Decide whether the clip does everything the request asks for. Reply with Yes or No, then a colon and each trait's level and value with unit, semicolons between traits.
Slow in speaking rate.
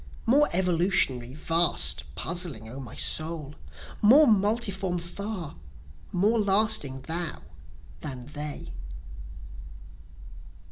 Yes: slow, 85 wpm